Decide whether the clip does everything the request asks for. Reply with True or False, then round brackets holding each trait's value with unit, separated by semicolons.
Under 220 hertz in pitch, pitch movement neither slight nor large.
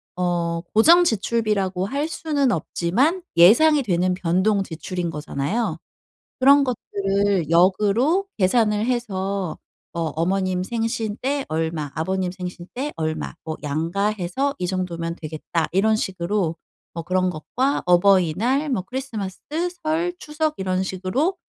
False (190 Hz; 5.8 semitones)